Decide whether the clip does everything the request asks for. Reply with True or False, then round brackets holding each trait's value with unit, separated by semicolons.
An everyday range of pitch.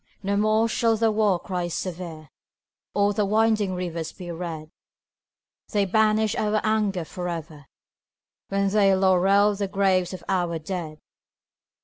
True (3.2 semitones)